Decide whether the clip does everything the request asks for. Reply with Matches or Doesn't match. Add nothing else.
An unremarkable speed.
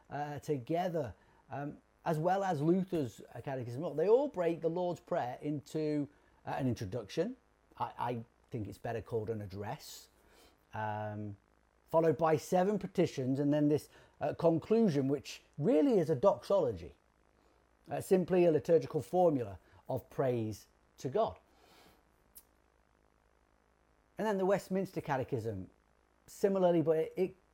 Doesn't match